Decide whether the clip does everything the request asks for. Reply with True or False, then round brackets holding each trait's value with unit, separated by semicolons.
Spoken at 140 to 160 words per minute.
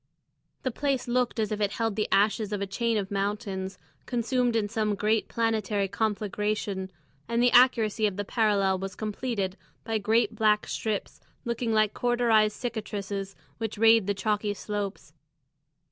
True (155 wpm)